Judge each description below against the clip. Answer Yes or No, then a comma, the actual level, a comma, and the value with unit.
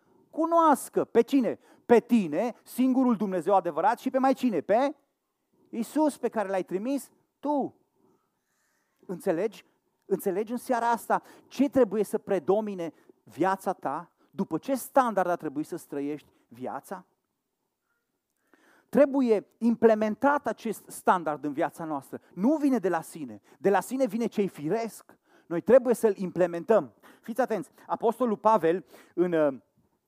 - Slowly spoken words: No, average, 130 wpm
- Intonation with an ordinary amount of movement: No, wide, 6.0 semitones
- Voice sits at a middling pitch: No, high, 220 Hz